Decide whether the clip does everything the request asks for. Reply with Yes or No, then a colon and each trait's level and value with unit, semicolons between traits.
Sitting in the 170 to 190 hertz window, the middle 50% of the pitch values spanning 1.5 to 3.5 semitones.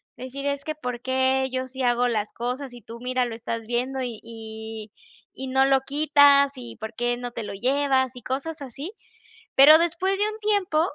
No: very high, 260 Hz; average, 2.8 semitones